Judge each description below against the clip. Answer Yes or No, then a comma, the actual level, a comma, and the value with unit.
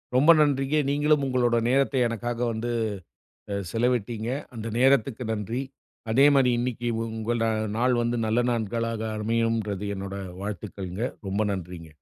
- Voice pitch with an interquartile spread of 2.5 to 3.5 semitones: Yes, average, 2.9 semitones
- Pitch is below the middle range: Yes, low, 115 Hz